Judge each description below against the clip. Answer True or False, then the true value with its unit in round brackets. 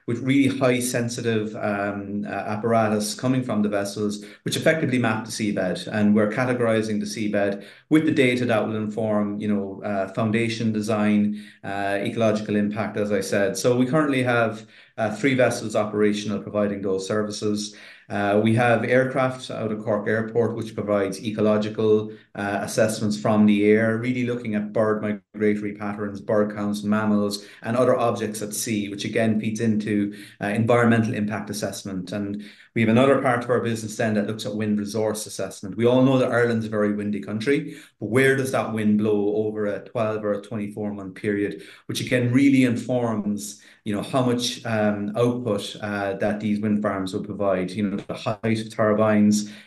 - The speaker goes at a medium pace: True (180 wpm)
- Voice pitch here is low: True (105 Hz)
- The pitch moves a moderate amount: False (2.1 semitones)